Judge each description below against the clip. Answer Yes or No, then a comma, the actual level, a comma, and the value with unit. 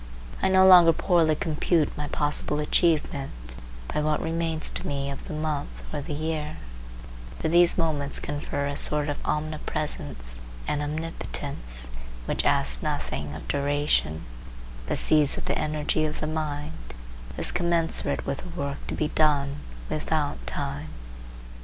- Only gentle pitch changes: Yes, narrow, 2.0 semitones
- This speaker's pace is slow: No, average, 145 wpm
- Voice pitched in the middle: Yes, medium, 150 Hz